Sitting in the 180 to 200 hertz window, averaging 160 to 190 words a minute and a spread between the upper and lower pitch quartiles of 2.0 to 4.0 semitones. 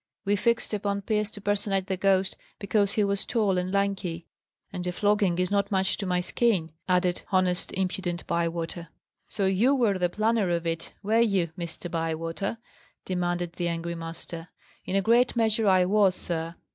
Yes: high, 190 Hz; average, 175 wpm; average, 2.8 semitones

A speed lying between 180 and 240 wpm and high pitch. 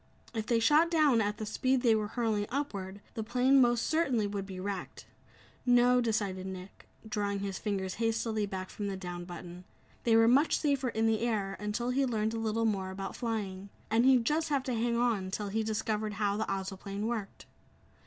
Yes: average, 195 wpm; high, 220 Hz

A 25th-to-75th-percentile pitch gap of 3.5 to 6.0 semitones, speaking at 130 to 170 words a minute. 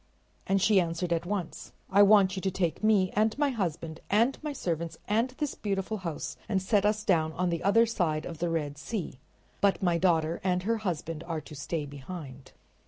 No: average, 4.1 semitones; average, 200 wpm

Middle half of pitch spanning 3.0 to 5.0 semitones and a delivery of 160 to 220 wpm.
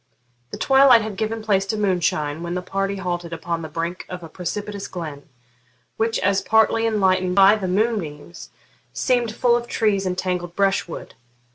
Yes: average, 3.7 semitones; average, 165 wpm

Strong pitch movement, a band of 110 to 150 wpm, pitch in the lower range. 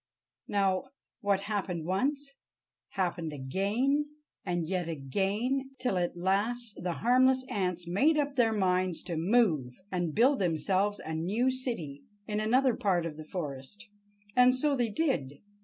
No: wide, 6.2 semitones; average, 140 wpm; high, 200 Hz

